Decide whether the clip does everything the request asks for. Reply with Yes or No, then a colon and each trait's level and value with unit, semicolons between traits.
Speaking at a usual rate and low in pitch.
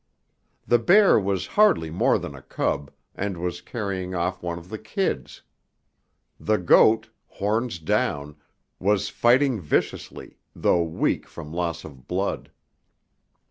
No: slow, 130 wpm; very low, 95 Hz